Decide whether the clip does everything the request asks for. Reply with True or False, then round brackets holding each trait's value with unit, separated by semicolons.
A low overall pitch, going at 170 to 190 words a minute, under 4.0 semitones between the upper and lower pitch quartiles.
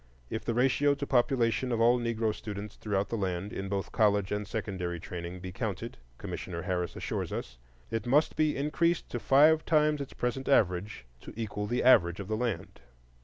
False (110 Hz; 185 wpm; 5.0 semitones)